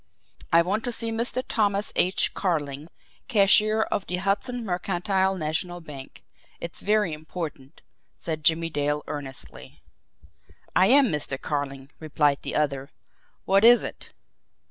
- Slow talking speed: Yes, slow, 130 wpm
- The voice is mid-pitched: Yes, medium, 175 Hz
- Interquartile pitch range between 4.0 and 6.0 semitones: Yes, wide, 5.6 semitones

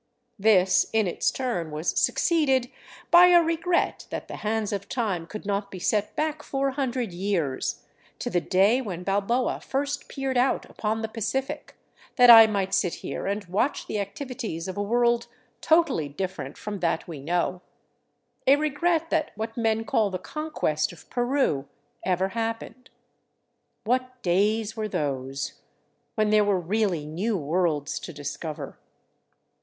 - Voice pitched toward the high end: Yes, high, 215 Hz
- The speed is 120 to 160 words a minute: Yes, average, 150 wpm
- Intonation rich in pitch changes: Yes, wide, 5.9 semitones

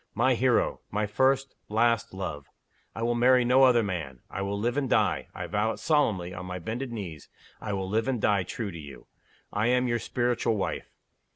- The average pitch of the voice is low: Yes, low, 110 Hz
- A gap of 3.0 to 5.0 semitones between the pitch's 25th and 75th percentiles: Yes, average, 4.3 semitones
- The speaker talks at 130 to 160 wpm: No, average, 200 wpm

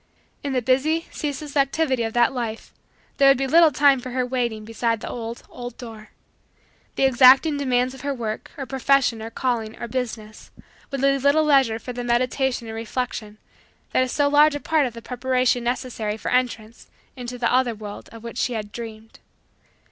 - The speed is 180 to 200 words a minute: Yes, average, 190 wpm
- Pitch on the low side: No, very high, 250 Hz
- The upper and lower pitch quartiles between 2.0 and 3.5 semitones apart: Yes, average, 2.9 semitones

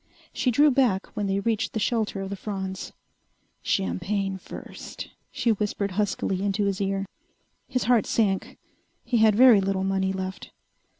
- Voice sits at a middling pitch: No, high, 200 Hz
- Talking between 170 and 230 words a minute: No, average, 155 wpm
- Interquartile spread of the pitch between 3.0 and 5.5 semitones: No, narrow, 2.5 semitones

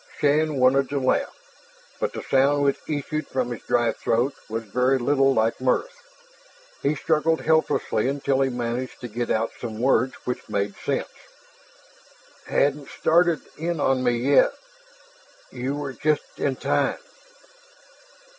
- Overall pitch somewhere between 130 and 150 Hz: Yes, low, 135 Hz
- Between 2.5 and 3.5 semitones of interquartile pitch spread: Yes, average, 3.0 semitones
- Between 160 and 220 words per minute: No, average, 145 wpm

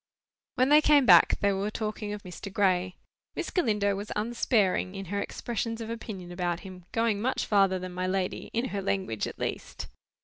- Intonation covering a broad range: No, average, 3.4 semitones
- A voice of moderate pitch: No, high, 200 Hz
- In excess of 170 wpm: Yes, average, 180 wpm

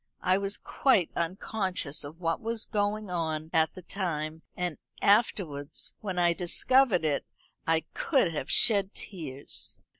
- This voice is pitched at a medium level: Yes, medium, 180 Hz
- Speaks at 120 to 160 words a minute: Yes, average, 140 wpm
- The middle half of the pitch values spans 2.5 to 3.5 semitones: No, average, 4.1 semitones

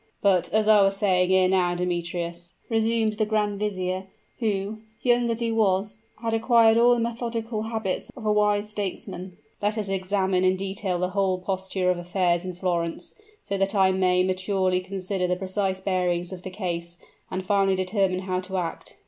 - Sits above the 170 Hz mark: Yes, high, 190 Hz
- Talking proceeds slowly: No, average, 180 wpm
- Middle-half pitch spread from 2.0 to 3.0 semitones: Yes, narrow, 2.4 semitones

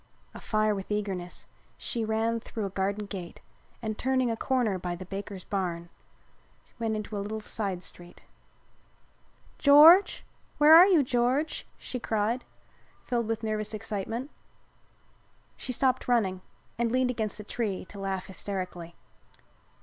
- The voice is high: Yes, high, 215 Hz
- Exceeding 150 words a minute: No, slow, 135 wpm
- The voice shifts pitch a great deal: No, average, 3.8 semitones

